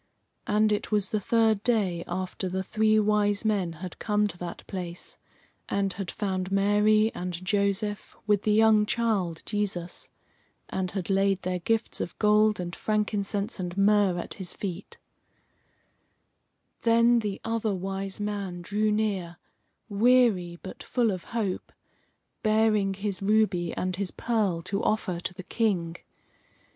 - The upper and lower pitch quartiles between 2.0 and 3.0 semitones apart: Yes, narrow, 2.6 semitones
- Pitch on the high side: Yes, high, 200 Hz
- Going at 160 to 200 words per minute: No, average, 145 wpm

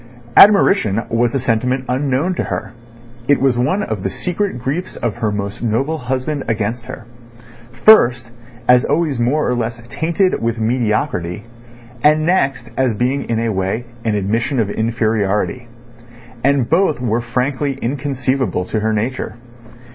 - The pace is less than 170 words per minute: Yes, average, 145 wpm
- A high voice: No, low, 125 Hz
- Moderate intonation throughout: Yes, average, 3.5 semitones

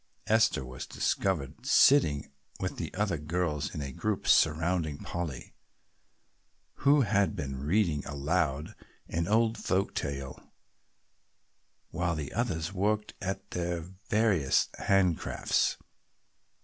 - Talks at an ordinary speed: No, slow, 110 wpm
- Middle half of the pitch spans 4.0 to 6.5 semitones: Yes, wide, 5.4 semitones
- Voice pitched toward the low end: Yes, very low, 85 Hz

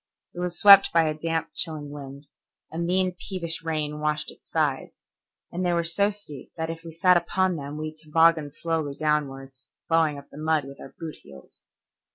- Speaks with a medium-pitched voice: Yes, medium, 160 Hz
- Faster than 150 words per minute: Yes, average, 190 wpm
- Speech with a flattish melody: Yes, narrow, 2.2 semitones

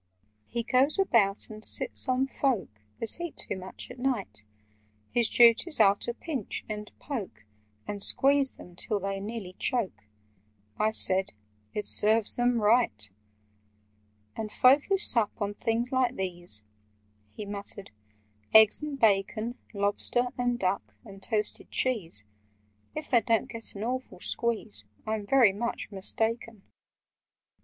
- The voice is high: Yes, high, 220 Hz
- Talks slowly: Yes, slow, 130 wpm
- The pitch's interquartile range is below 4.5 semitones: Yes, average, 3.7 semitones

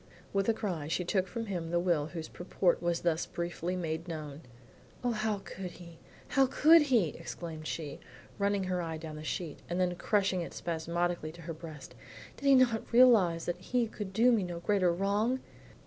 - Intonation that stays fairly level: No, average, 3.7 semitones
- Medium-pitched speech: Yes, medium, 175 Hz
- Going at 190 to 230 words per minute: Yes, average, 195 wpm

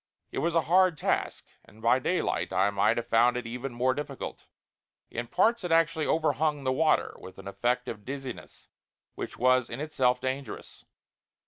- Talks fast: No, average, 175 wpm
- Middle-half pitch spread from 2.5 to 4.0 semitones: No, average, 4.6 semitones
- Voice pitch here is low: Yes, low, 130 Hz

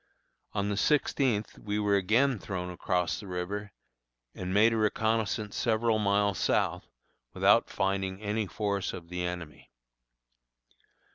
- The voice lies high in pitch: No, low, 100 Hz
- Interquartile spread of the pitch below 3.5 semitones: Yes, narrow, 2.6 semitones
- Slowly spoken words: Yes, slow, 130 wpm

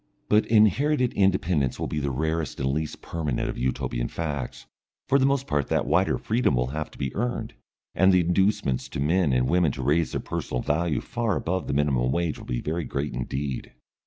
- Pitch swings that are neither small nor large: No, wide, 5.8 semitones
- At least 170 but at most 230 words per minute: Yes, average, 200 wpm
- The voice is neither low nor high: No, very low, 80 Hz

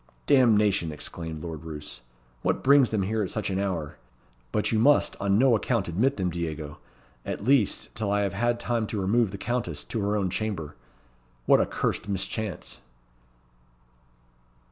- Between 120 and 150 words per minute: No, average, 165 wpm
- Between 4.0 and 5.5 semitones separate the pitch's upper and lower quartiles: Yes, average, 4.6 semitones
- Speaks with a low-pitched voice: Yes, low, 100 Hz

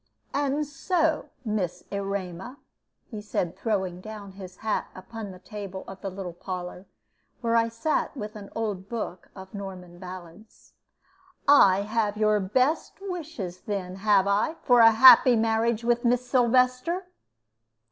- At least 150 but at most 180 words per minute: No, average, 140 wpm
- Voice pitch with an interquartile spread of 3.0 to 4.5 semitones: Yes, average, 4.1 semitones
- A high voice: Yes, high, 210 Hz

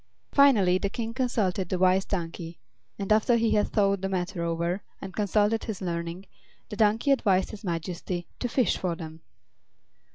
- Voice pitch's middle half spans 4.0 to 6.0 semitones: No, average, 3.6 semitones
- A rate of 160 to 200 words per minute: Yes, average, 165 wpm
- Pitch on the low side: No, high, 195 Hz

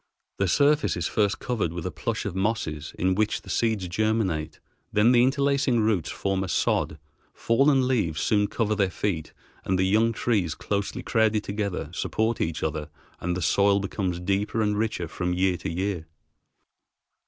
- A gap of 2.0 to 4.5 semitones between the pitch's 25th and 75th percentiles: Yes, average, 3.9 semitones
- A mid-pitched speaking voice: No, low, 100 Hz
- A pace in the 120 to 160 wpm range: No, average, 170 wpm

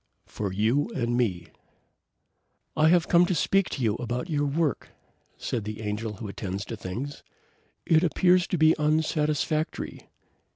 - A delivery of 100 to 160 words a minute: Yes, average, 150 wpm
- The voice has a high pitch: No, medium, 140 Hz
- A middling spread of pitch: No, wide, 6.7 semitones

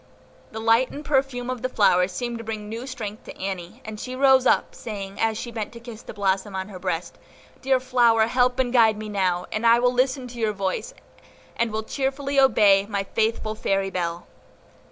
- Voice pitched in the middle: No, high, 225 Hz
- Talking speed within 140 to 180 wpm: No, average, 200 wpm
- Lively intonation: No, average, 4.0 semitones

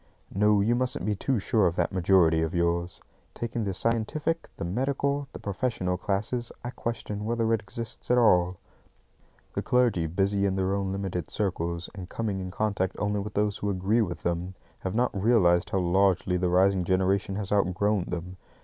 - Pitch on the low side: Yes, low, 100 Hz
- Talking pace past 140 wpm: Yes, average, 180 wpm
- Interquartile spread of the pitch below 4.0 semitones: Yes, average, 3.3 semitones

